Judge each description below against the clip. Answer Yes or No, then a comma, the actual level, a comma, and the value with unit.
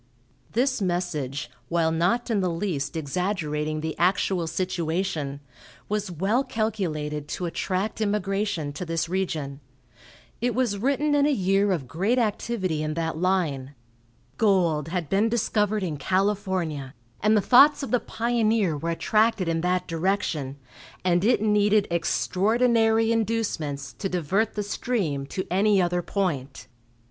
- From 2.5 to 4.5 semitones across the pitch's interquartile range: No, average, 4.9 semitones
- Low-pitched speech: No, medium, 185 Hz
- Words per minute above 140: No, slow, 135 wpm